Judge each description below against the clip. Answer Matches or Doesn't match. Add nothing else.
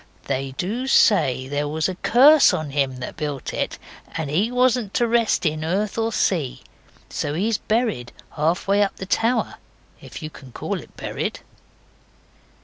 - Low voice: Doesn't match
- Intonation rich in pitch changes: Matches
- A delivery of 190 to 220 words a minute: Doesn't match